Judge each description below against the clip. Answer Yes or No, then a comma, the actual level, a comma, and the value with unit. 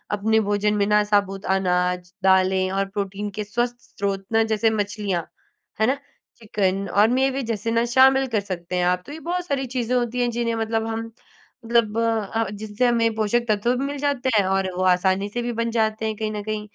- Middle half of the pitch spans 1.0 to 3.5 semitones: Yes, average, 2.9 semitones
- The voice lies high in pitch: Yes, high, 215 Hz